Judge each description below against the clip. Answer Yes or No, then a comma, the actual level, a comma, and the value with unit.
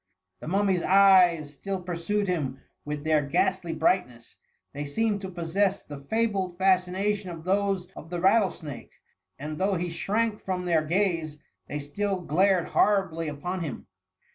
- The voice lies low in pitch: No, medium, 180 Hz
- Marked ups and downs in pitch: No, average, 3.7 semitones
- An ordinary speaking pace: Yes, average, 155 wpm